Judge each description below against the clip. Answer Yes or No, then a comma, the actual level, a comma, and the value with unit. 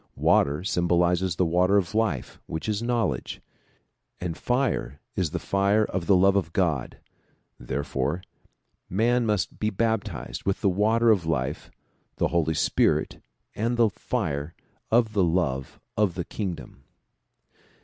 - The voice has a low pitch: Yes, very low, 95 Hz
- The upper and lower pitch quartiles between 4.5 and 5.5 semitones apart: Yes, average, 4.8 semitones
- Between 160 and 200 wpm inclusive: No, average, 140 wpm